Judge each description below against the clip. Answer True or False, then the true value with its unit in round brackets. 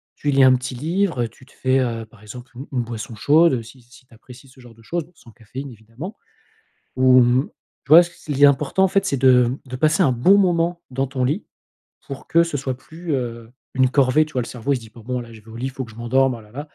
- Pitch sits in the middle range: False (130 Hz)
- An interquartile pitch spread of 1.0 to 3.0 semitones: False (3.8 semitones)